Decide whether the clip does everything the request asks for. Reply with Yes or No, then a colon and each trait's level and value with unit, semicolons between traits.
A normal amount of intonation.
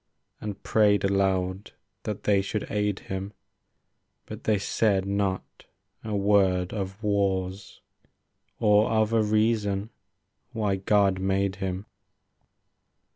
No: narrow, 1.5 semitones